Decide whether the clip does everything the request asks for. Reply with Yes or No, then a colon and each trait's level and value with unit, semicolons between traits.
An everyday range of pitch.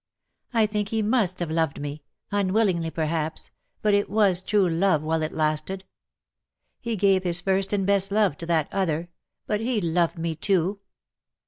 Yes: average, 3.9 semitones